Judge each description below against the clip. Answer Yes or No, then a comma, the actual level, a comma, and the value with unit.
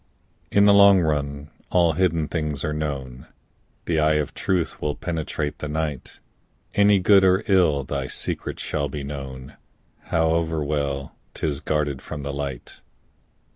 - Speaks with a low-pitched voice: Yes, very low, 75 Hz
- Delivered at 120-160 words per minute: Yes, average, 145 wpm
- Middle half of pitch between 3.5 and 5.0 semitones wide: No, average, 2.8 semitones